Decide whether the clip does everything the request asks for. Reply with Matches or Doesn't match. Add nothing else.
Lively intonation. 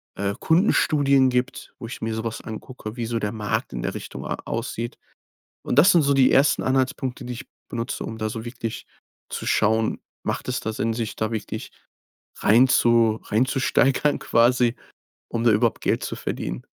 Doesn't match